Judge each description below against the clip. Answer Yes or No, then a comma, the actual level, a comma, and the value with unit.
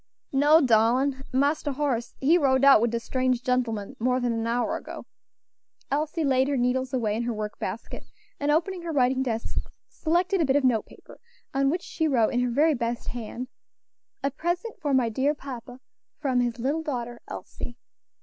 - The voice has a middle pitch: No, very high, 260 Hz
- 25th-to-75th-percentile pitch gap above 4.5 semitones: No, average, 3.3 semitones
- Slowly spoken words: No, average, 185 wpm